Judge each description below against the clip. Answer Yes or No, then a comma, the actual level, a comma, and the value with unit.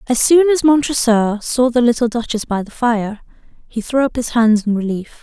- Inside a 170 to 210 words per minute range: Yes, fast, 205 wpm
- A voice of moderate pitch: No, high, 235 Hz